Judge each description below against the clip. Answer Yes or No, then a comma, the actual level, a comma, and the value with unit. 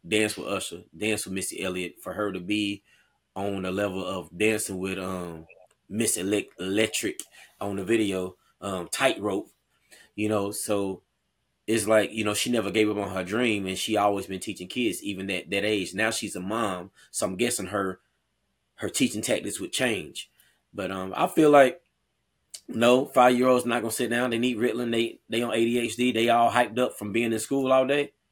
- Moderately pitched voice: No, low, 105 Hz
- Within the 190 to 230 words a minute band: Yes, average, 195 wpm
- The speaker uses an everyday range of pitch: Yes, average, 3.5 semitones